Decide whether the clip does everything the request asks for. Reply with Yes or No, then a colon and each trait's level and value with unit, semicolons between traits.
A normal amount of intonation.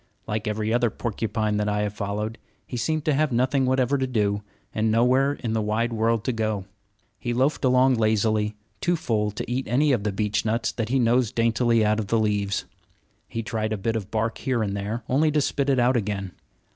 Yes: average, 3.1 semitones